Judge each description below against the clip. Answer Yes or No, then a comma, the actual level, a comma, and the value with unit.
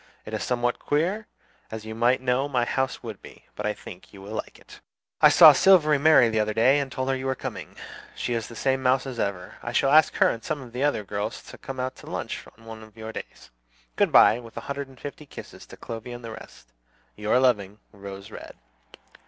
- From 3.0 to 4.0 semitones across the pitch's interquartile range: Yes, average, 3.4 semitones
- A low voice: Yes, low, 120 Hz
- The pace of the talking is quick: Yes, fast, 235 wpm